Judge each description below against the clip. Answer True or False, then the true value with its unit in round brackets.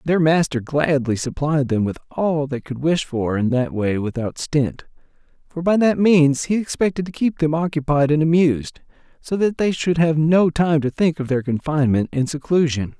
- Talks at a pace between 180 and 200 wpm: True (195 wpm)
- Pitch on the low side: False (150 Hz)